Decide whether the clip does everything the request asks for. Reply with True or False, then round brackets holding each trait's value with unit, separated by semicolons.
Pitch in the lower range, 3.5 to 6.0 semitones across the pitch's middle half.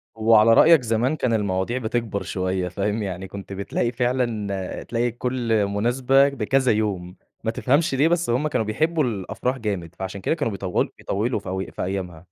True (110 Hz; 4.4 semitones)